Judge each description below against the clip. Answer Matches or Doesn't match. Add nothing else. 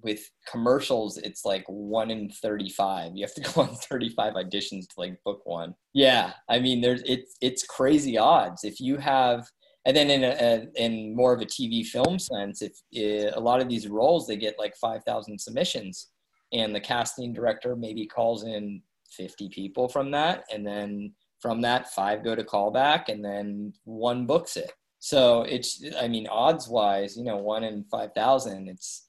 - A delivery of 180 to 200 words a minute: Matches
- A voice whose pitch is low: Matches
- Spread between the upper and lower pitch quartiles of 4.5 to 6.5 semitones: Doesn't match